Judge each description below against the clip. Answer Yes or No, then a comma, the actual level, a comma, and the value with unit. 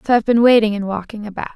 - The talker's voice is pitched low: No, high, 215 Hz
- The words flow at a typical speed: No, fast, 270 wpm